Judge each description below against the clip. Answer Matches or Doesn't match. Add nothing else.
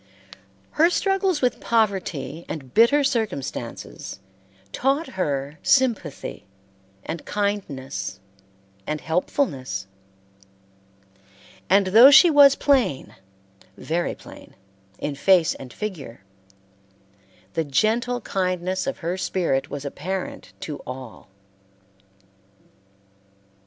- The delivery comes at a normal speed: Doesn't match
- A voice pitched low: Doesn't match